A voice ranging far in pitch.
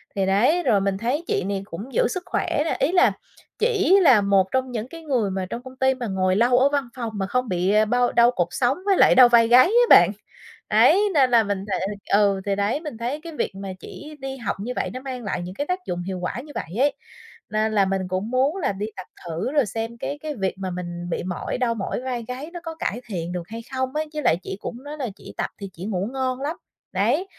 Yes: wide, 5.8 semitones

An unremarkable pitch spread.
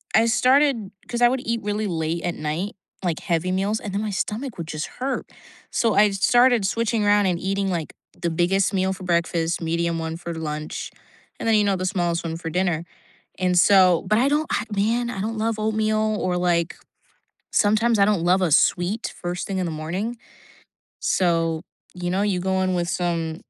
Yes: average, 4.0 semitones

